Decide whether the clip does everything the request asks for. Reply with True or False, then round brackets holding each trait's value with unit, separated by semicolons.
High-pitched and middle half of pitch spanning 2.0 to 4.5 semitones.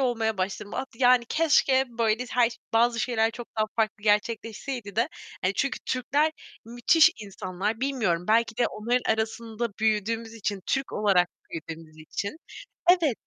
True (225 Hz; 2.9 semitones)